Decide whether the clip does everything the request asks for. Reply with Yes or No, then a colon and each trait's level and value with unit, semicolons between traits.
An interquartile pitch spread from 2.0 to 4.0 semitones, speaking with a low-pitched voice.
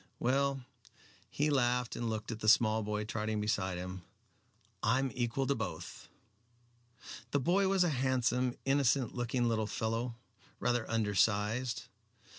Yes: average, 3.3 semitones; low, 120 Hz